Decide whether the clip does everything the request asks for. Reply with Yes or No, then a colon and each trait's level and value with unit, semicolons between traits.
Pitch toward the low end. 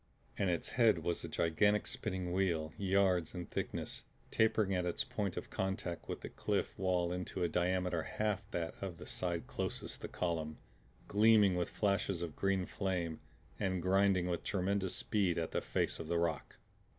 Yes: very low, 90 Hz